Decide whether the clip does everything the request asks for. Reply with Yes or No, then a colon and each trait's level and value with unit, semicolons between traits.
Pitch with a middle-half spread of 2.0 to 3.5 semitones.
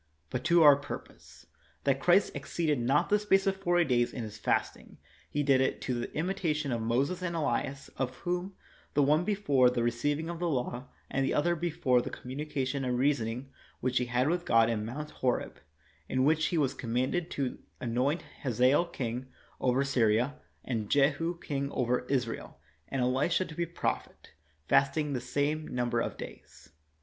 No: average, 4.2 semitones